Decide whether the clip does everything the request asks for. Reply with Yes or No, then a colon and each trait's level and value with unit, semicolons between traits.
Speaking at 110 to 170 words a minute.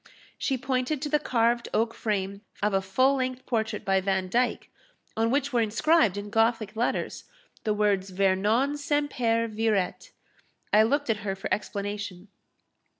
Yes: average, 150 wpm